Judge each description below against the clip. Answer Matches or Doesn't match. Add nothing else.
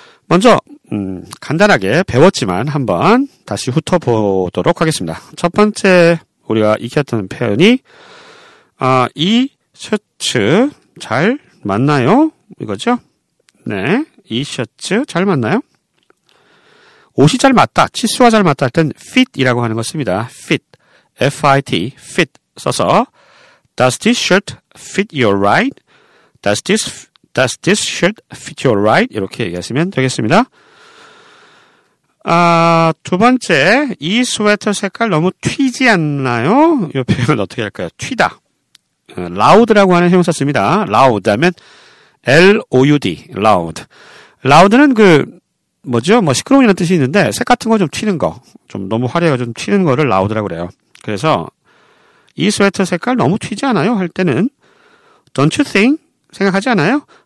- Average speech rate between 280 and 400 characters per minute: Matches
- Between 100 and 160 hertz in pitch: Doesn't match